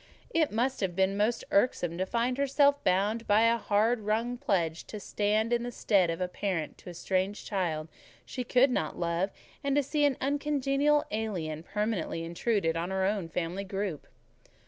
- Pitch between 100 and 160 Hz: No, high, 210 Hz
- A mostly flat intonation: No, average, 5.2 semitones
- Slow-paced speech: No, average, 180 wpm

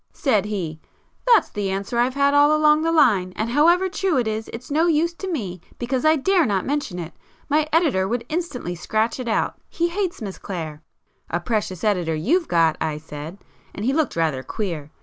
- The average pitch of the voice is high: Yes, high, 235 Hz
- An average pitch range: No, wide, 8.9 semitones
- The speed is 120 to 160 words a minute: No, average, 190 wpm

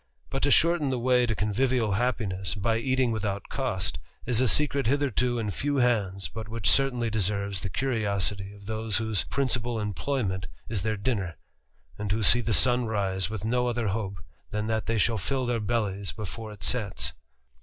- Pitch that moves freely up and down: No, average, 3.5 semitones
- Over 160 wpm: Yes, average, 180 wpm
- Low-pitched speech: Yes, low, 110 Hz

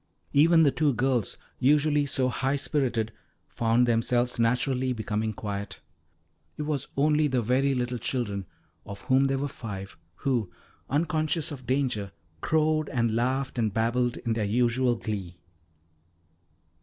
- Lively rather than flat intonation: No, average, 3.6 semitones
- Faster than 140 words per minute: No, slow, 135 wpm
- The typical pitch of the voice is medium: No, low, 125 Hz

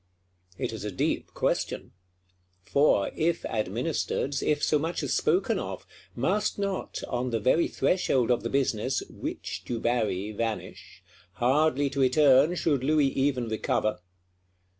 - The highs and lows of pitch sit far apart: No, average, 4.8 semitones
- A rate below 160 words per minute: Yes, slow, 135 wpm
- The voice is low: Yes, low, 130 Hz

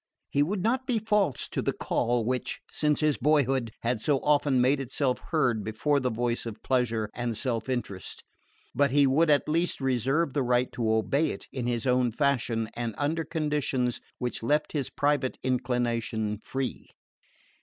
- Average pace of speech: Yes, average, 170 wpm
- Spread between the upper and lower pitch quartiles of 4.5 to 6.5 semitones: No, average, 3.6 semitones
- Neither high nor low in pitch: No, low, 130 Hz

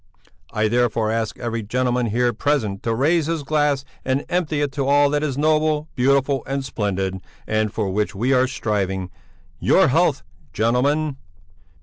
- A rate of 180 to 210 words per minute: No, average, 155 wpm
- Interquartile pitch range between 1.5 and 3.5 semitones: No, average, 4.9 semitones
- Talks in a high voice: No, low, 130 Hz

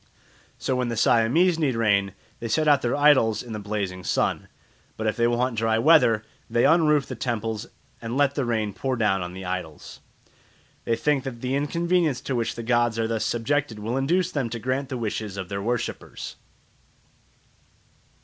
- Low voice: Yes, low, 120 Hz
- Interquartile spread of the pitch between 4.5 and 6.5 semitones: No, average, 3.9 semitones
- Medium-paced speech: Yes, average, 185 wpm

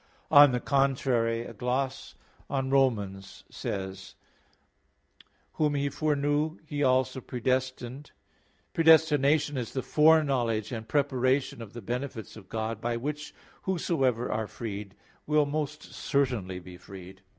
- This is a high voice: No, low, 130 Hz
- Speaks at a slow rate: Yes, slow, 125 wpm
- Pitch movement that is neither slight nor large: Yes, average, 4.1 semitones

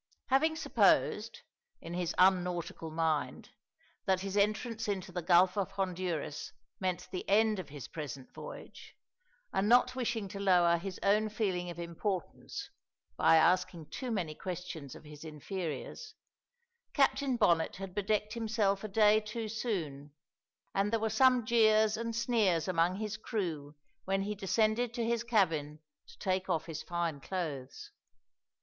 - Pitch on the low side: No, high, 190 Hz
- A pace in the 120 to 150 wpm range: Yes, average, 145 wpm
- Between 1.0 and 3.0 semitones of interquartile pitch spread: No, average, 4.3 semitones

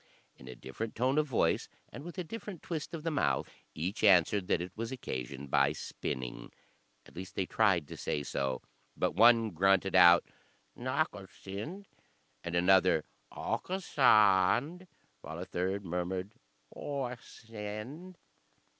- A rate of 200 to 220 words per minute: No, average, 145 wpm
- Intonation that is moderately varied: No, wide, 7.2 semitones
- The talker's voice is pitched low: Yes, low, 100 Hz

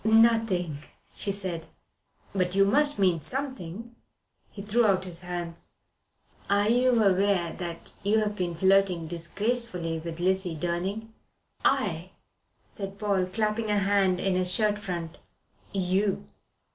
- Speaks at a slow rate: Yes, slow, 125 wpm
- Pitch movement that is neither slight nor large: Yes, average, 3.1 semitones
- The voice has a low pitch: No, high, 195 Hz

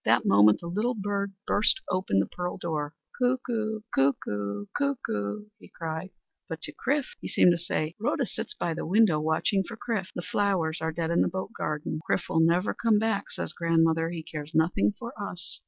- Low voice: No, medium, 175 Hz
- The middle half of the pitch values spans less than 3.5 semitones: No, average, 4.8 semitones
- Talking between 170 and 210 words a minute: Yes, average, 190 wpm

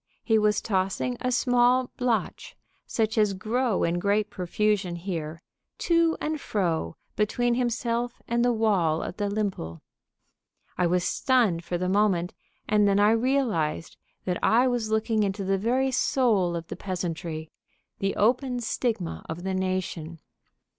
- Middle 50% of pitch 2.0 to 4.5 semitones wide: No, average, 5.1 semitones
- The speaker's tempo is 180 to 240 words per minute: No, average, 145 wpm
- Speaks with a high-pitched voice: Yes, high, 210 Hz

